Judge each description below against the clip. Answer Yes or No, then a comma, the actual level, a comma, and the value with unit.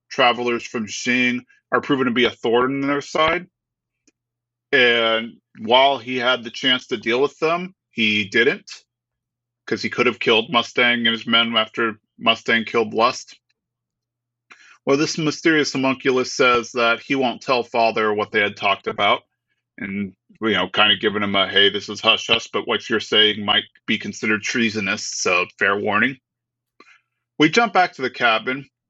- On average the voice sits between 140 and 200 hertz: No, low, 120 Hz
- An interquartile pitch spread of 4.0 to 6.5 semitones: No, narrow, 2.5 semitones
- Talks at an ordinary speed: Yes, average, 170 wpm